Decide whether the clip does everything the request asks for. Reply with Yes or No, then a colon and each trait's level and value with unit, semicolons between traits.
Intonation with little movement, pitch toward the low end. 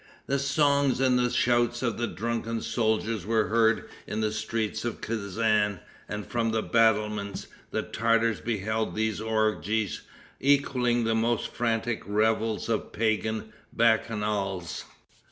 Yes: narrow, 1.6 semitones; low, 110 Hz